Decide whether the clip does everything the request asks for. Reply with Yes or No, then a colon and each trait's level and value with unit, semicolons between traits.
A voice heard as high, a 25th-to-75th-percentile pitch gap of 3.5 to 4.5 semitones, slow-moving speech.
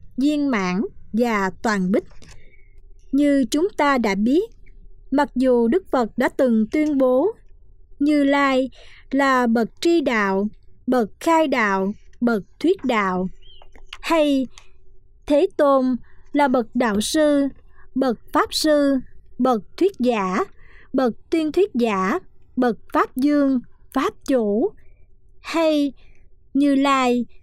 Yes: very high, 265 Hz; average, 3.8 semitones; slow, 120 wpm